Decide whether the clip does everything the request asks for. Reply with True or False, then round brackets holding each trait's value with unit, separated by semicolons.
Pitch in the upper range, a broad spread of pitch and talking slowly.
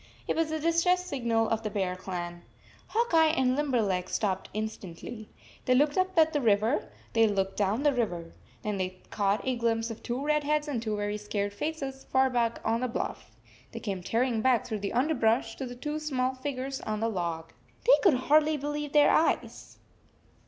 False (240 Hz; 5.9 semitones; 190 wpm)